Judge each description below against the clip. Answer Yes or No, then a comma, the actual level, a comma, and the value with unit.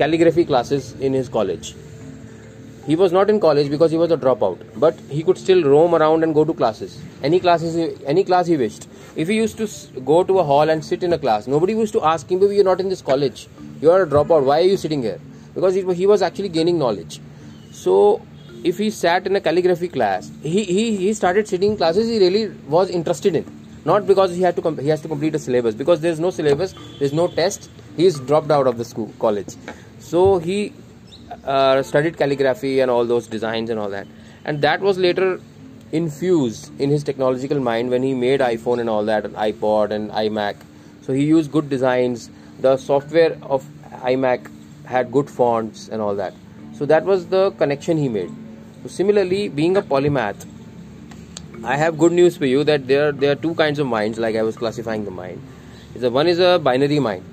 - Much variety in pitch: Yes, wide, 6.5 semitones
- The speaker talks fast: Yes, fast, 210 wpm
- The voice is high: No, medium, 150 Hz